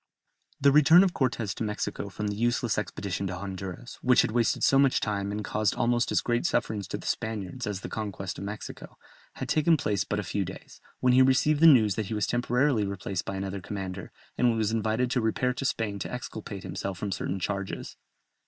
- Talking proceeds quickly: Yes, fast, 210 wpm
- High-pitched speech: No, low, 110 Hz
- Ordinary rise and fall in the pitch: Yes, average, 3.9 semitones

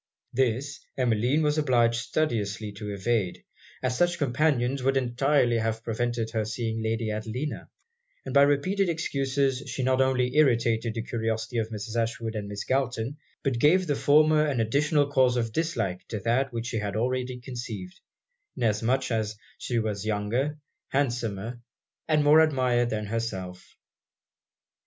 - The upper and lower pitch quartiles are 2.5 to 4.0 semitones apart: Yes, average, 3.7 semitones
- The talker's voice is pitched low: Yes, low, 120 Hz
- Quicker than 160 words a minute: No, average, 145 wpm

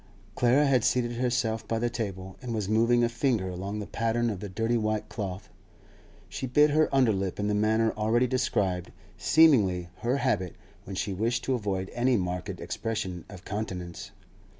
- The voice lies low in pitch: Yes, low, 110 Hz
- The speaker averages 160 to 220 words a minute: Yes, average, 175 wpm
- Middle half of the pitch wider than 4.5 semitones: No, average, 3.9 semitones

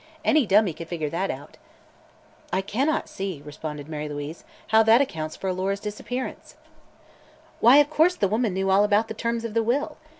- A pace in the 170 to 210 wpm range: Yes, average, 180 wpm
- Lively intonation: Yes, wide, 5.8 semitones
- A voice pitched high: Yes, high, 200 Hz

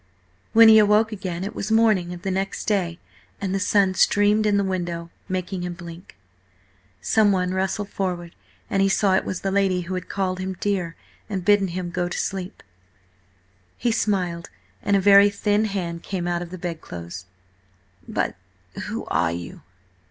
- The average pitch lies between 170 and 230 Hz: Yes, high, 190 Hz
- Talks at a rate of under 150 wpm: No, average, 175 wpm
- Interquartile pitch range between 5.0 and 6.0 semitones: No, narrow, 2.4 semitones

